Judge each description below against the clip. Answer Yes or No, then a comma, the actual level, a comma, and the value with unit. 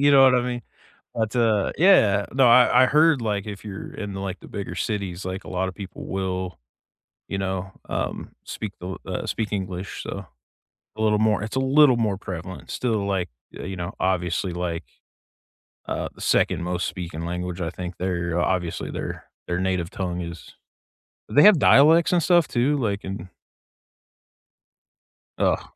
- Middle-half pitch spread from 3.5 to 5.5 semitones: Yes, average, 4.6 semitones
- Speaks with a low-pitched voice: Yes, very low, 95 Hz